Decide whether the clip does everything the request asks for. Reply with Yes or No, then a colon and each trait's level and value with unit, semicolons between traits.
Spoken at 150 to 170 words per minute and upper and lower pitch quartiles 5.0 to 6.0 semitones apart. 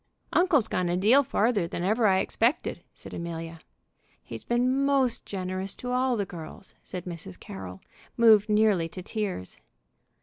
Yes: average, 155 wpm; wide, 5.6 semitones